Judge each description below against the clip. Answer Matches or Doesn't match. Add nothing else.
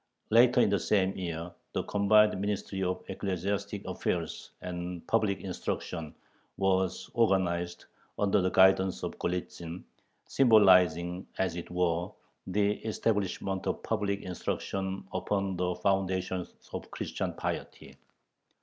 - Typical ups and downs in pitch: Doesn't match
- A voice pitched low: Matches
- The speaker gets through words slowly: Matches